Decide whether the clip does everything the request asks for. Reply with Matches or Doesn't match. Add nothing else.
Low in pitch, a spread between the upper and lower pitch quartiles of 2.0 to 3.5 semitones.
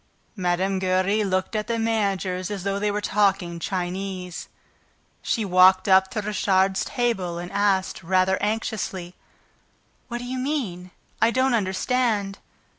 Doesn't match